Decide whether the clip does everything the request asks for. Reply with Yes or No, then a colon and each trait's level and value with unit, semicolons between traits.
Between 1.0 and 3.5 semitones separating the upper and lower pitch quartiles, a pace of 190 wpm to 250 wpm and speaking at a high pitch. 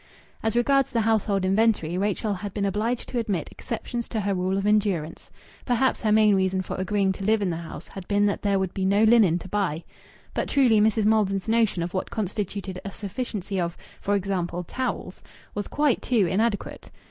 Yes: average, 2.8 semitones; average, 195 wpm; high, 205 Hz